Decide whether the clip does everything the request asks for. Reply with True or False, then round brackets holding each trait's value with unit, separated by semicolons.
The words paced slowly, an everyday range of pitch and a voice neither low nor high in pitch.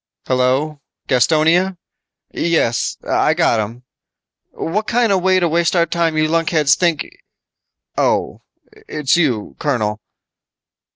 True (110 wpm; 4.9 semitones; 155 Hz)